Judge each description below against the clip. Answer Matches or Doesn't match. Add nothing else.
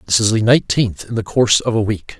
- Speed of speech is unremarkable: Doesn't match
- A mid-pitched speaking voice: Doesn't match